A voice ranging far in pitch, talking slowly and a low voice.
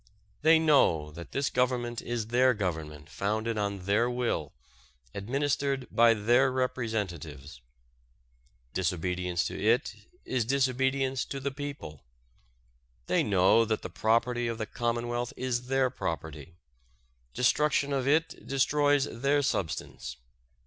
Yes: wide, 5.8 semitones; slow, 120 wpm; low, 120 Hz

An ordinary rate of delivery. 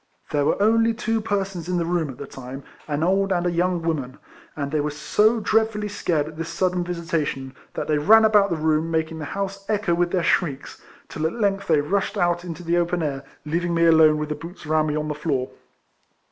No: fast, 225 wpm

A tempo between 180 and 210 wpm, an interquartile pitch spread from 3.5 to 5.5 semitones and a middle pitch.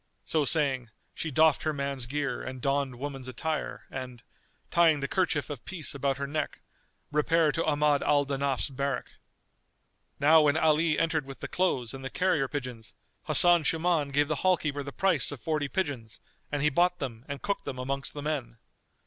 No: average, 185 wpm; narrow, 2.6 semitones; medium, 145 Hz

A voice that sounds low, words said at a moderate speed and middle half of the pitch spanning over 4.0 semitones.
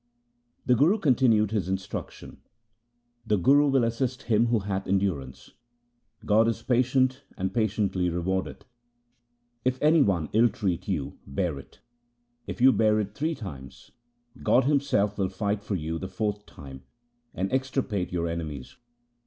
Yes: low, 105 Hz; average, 150 wpm; average, 4.9 semitones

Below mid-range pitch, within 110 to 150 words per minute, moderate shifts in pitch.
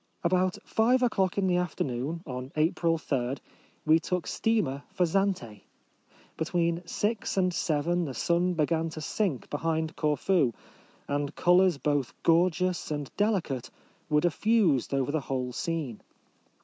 No: medium, 165 Hz; average, 140 wpm; average, 4.1 semitones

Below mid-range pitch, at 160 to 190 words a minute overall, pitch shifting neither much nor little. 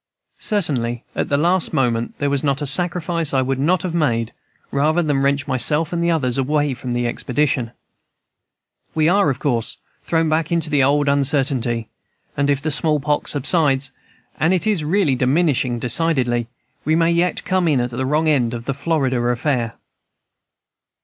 No: medium, 145 Hz; average, 170 wpm; average, 4.0 semitones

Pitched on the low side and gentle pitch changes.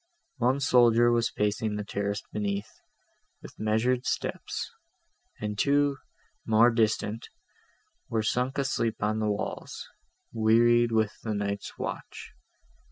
Yes: low, 110 Hz; narrow, 2.2 semitones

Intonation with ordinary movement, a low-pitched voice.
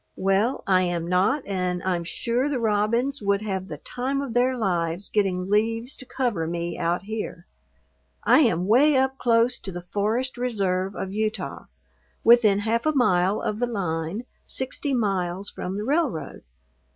No: average, 5.0 semitones; high, 210 Hz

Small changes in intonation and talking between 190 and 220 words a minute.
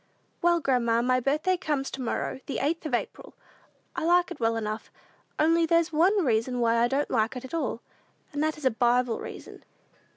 No: wide, 5.5 semitones; average, 195 wpm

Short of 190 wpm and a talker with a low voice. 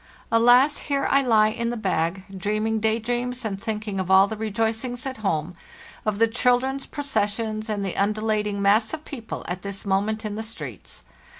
No: average, 180 wpm; high, 220 Hz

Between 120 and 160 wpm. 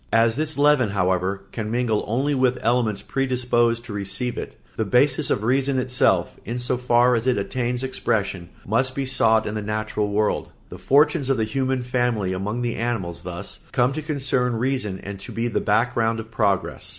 No: average, 185 wpm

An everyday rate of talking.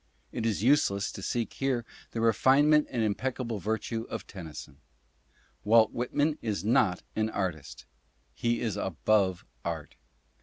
No: slow, 130 wpm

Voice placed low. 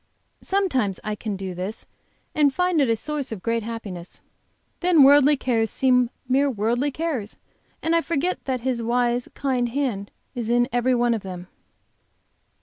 No: high, 245 Hz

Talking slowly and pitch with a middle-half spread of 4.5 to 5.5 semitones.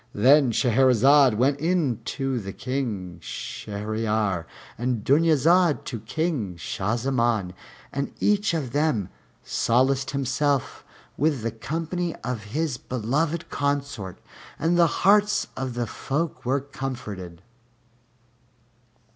Yes: slow, 105 wpm; average, 5.1 semitones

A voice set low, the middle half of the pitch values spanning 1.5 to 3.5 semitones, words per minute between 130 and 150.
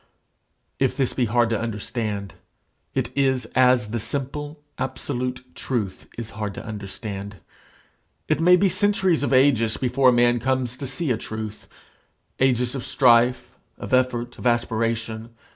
Yes: low, 120 Hz; average, 2.9 semitones; average, 145 wpm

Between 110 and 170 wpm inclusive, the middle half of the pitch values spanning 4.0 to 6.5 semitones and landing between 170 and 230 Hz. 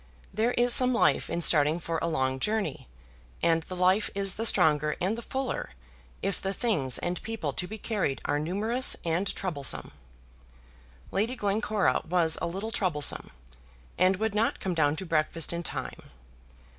Yes: average, 165 wpm; average, 5.2 semitones; medium, 185 Hz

